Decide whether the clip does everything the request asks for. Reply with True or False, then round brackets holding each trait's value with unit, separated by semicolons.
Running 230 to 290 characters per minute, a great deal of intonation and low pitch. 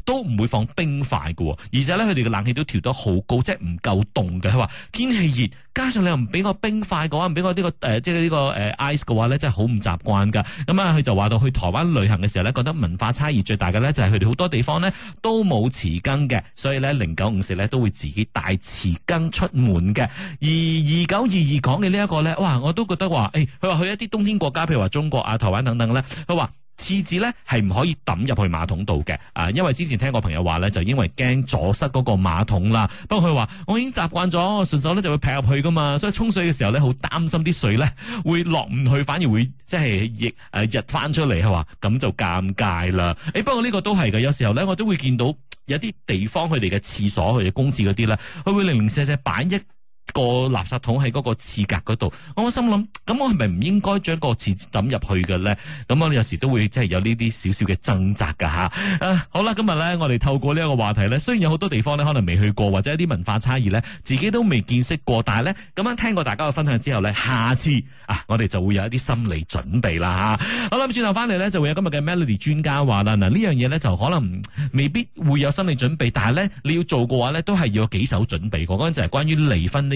False (370 characters per minute; 7.7 semitones; 130 Hz)